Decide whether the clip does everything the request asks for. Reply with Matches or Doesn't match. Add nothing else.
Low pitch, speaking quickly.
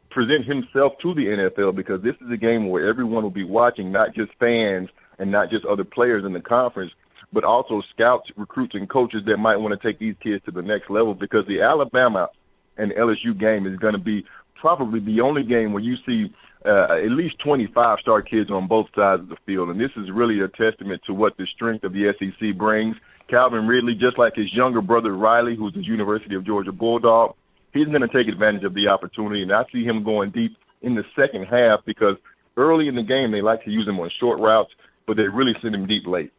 Matches